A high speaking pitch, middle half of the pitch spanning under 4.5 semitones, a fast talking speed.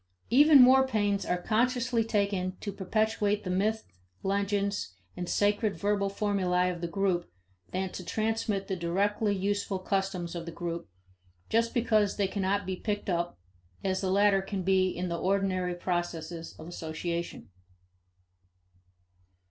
No: high, 195 Hz; narrow, 2.5 semitones; average, 140 wpm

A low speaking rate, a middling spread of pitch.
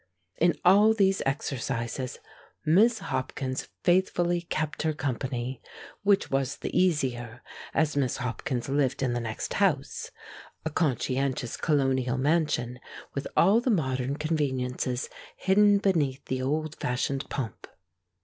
Yes: slow, 120 wpm; average, 4.8 semitones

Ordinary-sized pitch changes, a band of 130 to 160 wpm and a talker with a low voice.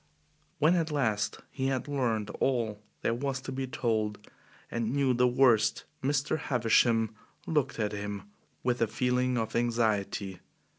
Yes: average, 3.4 semitones; average, 145 wpm; low, 120 Hz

